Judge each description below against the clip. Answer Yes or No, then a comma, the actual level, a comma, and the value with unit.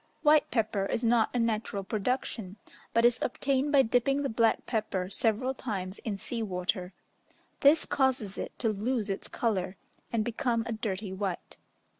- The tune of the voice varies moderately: Yes, average, 3.9 semitones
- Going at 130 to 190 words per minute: Yes, average, 160 wpm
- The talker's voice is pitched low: No, high, 225 Hz